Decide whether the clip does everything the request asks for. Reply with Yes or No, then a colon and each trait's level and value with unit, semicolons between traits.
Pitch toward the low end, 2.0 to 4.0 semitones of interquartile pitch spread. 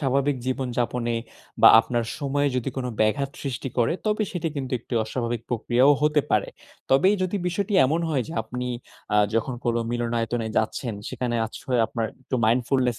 Yes: low, 125 Hz; average, 3.0 semitones